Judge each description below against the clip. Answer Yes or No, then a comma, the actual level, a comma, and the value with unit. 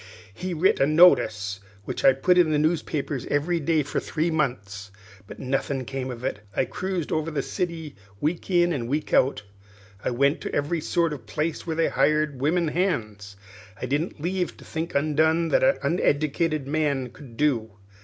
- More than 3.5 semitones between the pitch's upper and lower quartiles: Yes, average, 3.9 semitones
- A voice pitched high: No, medium, 150 Hz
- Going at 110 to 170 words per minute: No, average, 180 wpm